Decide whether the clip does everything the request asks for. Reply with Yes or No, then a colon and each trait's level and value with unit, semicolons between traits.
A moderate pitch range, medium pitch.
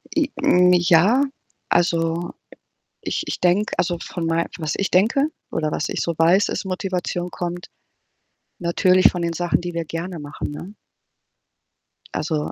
No: narrow, 1.8 semitones; medium, 175 Hz